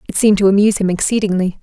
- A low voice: No, high, 200 Hz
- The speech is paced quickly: Yes, fast, 220 wpm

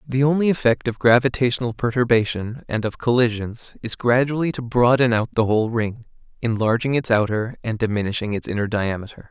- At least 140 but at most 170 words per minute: Yes, average, 160 wpm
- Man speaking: Yes, male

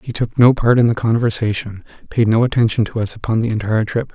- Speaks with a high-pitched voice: No, low, 110 Hz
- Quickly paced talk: Yes, fast, 230 wpm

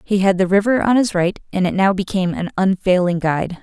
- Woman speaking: Yes, female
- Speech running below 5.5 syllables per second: No, 6.0 syllables/s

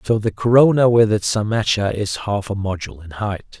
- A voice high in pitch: No, low, 105 Hz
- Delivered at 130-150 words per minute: No, average, 200 wpm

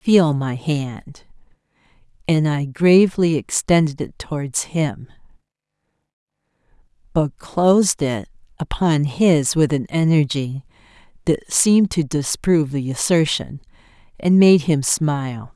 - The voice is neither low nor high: Yes, medium, 150 Hz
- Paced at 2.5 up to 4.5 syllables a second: Yes, 3.9 syllables/s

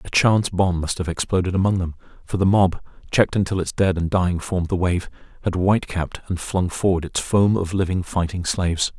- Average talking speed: No, fast, 215 wpm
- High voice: No, very low, 90 Hz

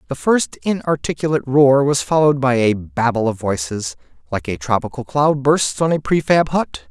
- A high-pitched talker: No, low, 135 Hz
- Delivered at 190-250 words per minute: No, average, 165 wpm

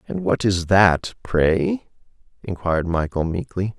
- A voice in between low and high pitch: No, very low, 90 Hz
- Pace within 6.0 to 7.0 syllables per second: No, 4.0 syllables/s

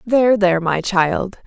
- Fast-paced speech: No, average, 165 wpm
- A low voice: No, high, 195 Hz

